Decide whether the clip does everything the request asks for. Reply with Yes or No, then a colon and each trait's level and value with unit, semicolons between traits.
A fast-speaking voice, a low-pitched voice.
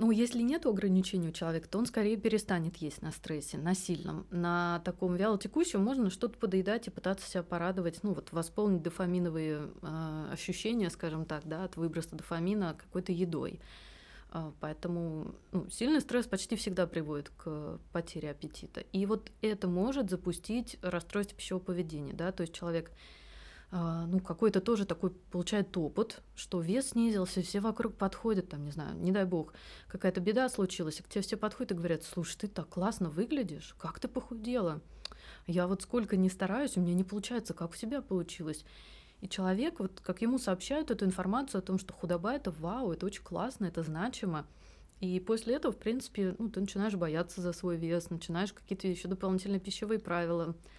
No: fast, 175 wpm; medium, 185 Hz